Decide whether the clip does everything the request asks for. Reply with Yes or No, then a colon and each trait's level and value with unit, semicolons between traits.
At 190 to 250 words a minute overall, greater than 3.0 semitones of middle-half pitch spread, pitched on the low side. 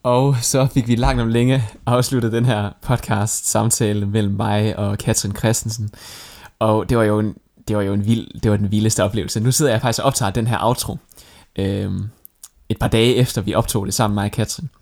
No: average, 215 wpm; narrow, 2.5 semitones; low, 110 Hz